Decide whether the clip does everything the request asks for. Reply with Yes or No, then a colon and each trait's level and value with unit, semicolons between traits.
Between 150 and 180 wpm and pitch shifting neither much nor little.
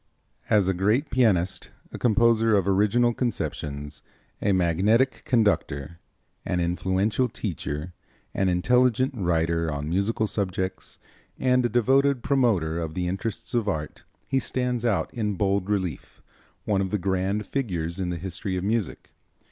No: average, 140 wpm; average, 4.9 semitones